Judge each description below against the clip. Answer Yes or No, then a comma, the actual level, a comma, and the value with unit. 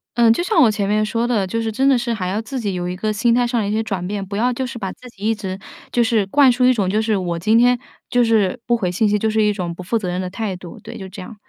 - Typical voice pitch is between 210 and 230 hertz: Yes, high, 215 Hz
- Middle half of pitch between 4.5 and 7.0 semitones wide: No, average, 3.6 semitones